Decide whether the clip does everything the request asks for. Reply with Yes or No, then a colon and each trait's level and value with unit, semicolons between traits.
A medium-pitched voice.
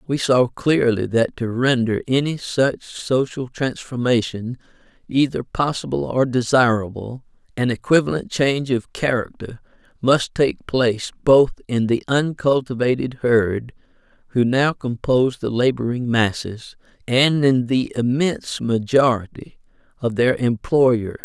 No: low, 125 Hz